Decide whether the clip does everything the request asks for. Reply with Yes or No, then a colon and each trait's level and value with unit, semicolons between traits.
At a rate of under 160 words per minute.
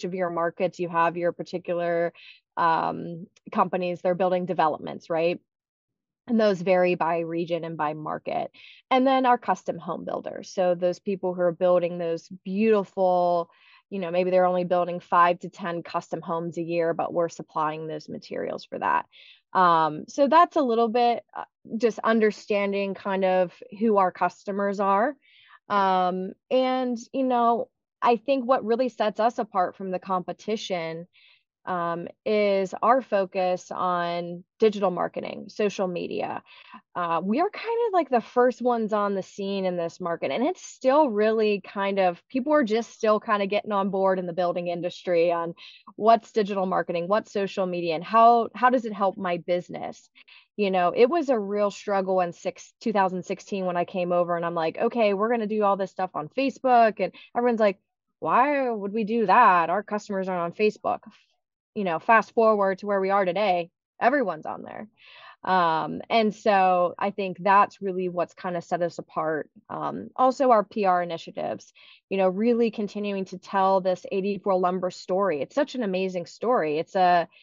No: average, 180 wpm